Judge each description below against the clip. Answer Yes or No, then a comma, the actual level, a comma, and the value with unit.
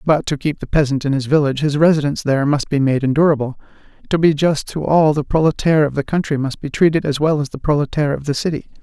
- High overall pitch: No, medium, 145 Hz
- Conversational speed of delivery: No, fast, 245 wpm